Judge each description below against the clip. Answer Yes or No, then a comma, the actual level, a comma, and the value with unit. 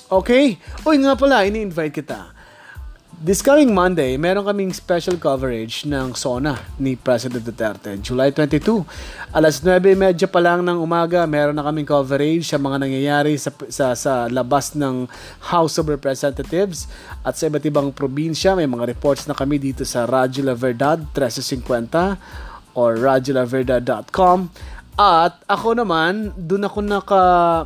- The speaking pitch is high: No, medium, 150 Hz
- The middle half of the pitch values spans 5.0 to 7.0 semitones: Yes, average, 5.3 semitones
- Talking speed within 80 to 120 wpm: No, average, 140 wpm